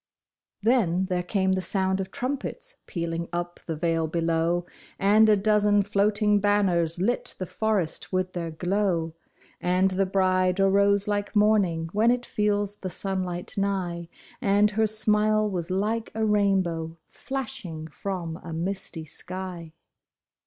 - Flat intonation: No, average, 3.2 semitones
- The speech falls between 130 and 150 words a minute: Yes, average, 140 wpm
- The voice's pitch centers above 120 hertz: Yes, high, 190 Hz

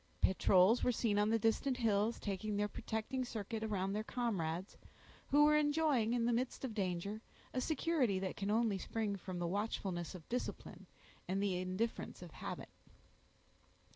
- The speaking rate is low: No, average, 165 wpm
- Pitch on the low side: No, high, 215 Hz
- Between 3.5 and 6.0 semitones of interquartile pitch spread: Yes, average, 3.8 semitones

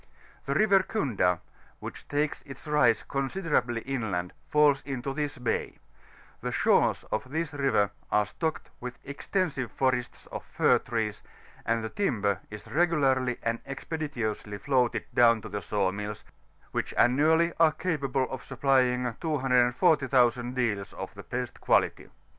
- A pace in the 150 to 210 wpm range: No, slow, 135 wpm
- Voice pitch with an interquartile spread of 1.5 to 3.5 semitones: No, average, 4.3 semitones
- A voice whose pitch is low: Yes, low, 130 Hz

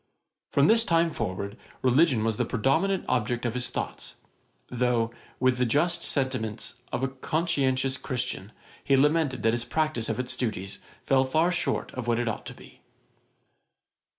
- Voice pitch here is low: Yes, low, 130 Hz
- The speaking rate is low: No, average, 160 wpm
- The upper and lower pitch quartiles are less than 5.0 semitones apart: Yes, average, 4.5 semitones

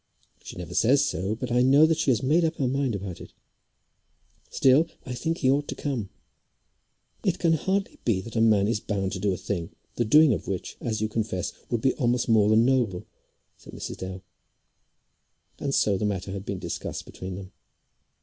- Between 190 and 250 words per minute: Yes, average, 200 wpm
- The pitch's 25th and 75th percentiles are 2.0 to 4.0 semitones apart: No, wide, 5.5 semitones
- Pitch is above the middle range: No, low, 115 Hz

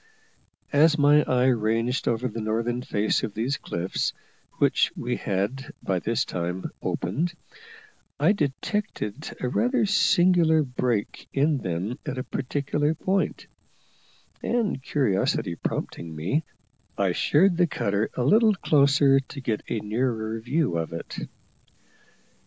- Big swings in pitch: Yes, wide, 6.0 semitones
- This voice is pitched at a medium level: No, low, 130 Hz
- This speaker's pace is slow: Yes, slow, 130 wpm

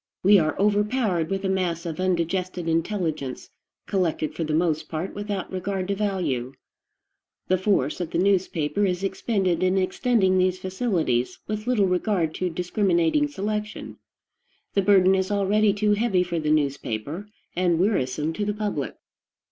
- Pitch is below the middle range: No, medium, 185 Hz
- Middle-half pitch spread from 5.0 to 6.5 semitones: No, average, 3.5 semitones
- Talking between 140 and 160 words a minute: Yes, average, 150 wpm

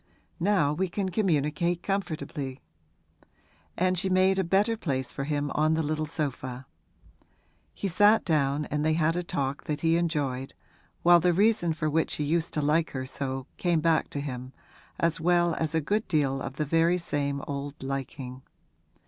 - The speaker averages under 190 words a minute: Yes, average, 175 wpm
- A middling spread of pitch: Yes, average, 3.6 semitones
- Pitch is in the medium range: Yes, medium, 155 Hz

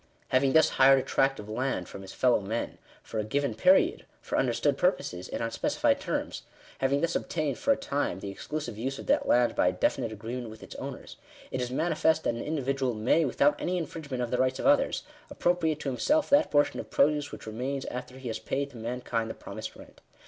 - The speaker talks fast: Yes, fast, 220 wpm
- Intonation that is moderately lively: Yes, average, 4.2 semitones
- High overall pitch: No, low, 130 Hz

